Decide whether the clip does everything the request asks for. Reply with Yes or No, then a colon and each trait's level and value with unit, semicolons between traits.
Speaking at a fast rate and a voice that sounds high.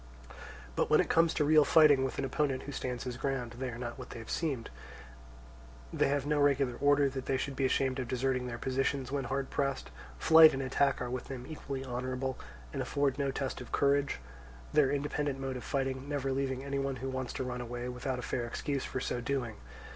No: fast, 215 wpm; low, 135 Hz